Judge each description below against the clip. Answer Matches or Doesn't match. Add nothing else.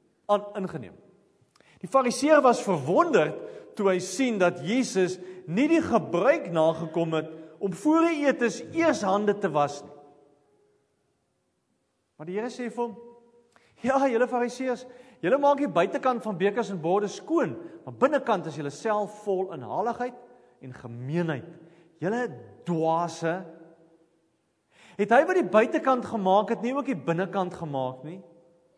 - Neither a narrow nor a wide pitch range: Doesn't match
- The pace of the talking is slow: Doesn't match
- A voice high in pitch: Matches